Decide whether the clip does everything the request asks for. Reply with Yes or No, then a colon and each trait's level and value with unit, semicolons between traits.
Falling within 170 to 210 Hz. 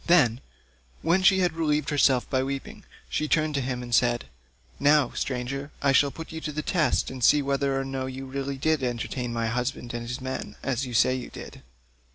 No: low, 135 Hz